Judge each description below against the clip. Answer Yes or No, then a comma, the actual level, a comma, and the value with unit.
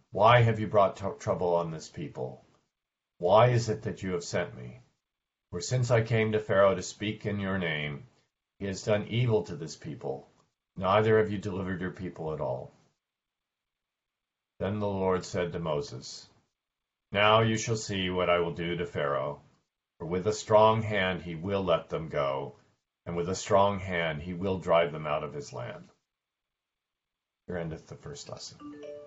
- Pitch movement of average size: Yes, average, 3.8 semitones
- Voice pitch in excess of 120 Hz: No, low, 100 Hz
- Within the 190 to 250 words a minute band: No, average, 180 wpm